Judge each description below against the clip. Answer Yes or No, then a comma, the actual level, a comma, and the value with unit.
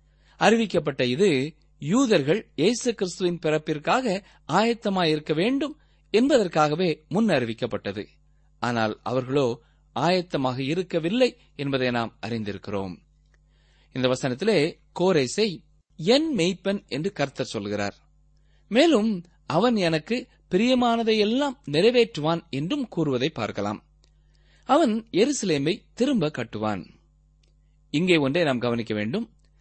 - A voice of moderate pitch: Yes, medium, 150 Hz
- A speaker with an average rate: Yes, average, 85 wpm